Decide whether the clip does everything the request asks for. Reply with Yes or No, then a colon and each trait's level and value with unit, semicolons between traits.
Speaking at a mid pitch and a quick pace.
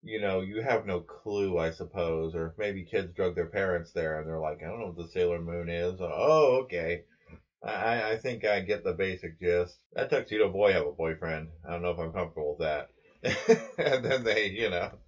No: low, 100 Hz; fast, 225 wpm